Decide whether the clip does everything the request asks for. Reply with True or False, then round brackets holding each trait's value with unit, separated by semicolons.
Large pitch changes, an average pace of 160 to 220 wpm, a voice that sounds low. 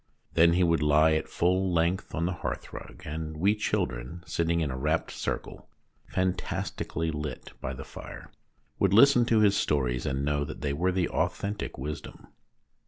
False (3.8 semitones; 170 wpm; 80 Hz)